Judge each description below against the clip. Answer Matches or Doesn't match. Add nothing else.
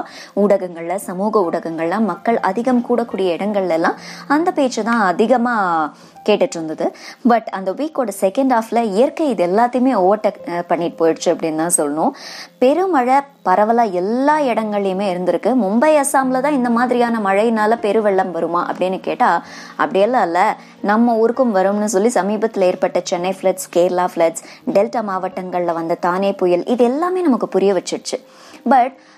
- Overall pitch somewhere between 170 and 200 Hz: Doesn't match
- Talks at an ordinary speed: Doesn't match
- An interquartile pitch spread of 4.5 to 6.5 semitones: Matches